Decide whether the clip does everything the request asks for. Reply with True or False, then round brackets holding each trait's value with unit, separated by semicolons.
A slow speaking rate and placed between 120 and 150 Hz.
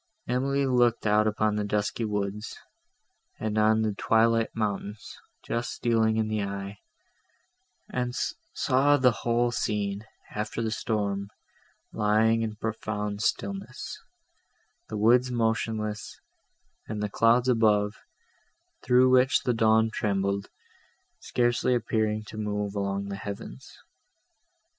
False (115 wpm; 110 Hz)